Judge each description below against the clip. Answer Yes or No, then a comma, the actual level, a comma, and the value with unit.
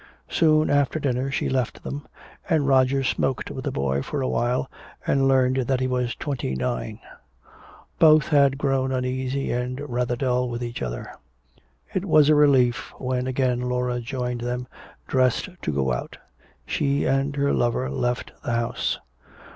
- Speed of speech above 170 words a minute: No, average, 160 wpm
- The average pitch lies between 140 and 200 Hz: No, low, 130 Hz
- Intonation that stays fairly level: Yes, narrow, 2.0 semitones